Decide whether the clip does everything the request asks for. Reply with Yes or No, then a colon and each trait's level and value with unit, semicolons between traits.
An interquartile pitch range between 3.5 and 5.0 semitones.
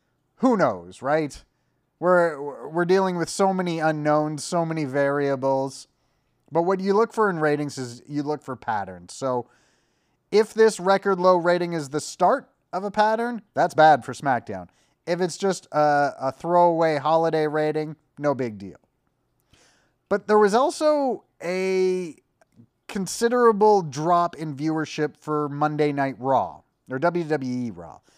Yes: average, 4.5 semitones